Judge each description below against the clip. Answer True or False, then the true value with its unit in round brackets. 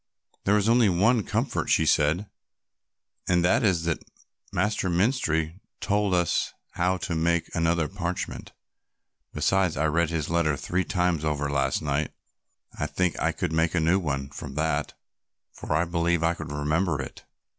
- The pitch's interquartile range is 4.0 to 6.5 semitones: False (3.1 semitones)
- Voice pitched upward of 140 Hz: False (85 Hz)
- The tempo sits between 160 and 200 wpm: True (165 wpm)